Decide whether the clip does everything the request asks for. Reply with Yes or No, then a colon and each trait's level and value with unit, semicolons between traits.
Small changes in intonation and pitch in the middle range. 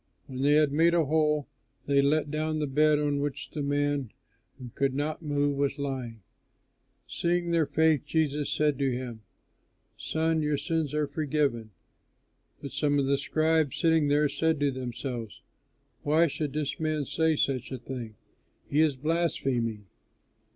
Yes: narrow, 2.3 semitones; medium, 145 Hz